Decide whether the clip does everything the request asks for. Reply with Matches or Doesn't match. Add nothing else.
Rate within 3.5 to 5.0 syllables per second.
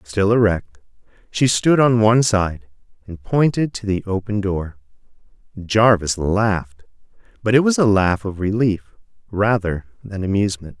Matches